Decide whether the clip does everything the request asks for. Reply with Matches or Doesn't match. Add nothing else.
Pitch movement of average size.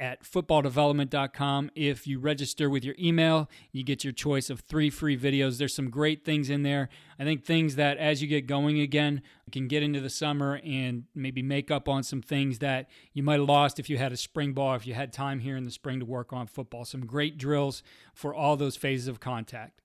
Doesn't match